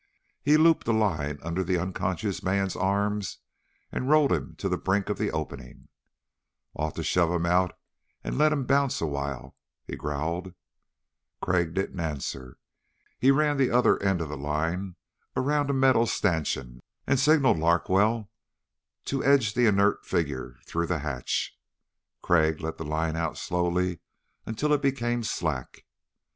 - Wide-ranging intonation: Yes, wide, 6.9 semitones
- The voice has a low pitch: Yes, very low, 90 Hz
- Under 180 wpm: Yes, average, 155 wpm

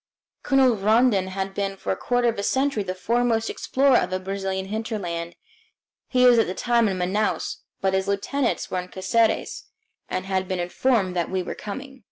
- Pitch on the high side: Yes, high, 200 Hz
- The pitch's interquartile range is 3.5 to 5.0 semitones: Yes, average, 4.1 semitones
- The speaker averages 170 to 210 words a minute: Yes, average, 190 wpm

